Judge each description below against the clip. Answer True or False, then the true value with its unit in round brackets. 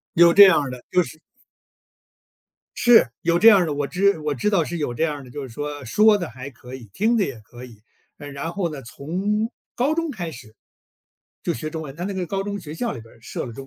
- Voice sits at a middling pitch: True (160 Hz)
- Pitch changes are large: True (6.8 semitones)